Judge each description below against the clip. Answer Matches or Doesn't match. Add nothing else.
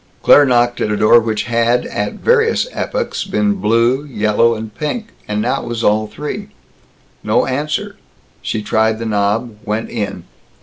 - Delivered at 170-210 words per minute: Doesn't match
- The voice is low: Matches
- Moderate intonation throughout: Matches